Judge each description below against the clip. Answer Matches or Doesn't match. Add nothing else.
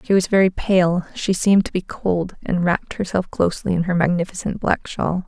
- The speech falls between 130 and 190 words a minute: Doesn't match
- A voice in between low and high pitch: Matches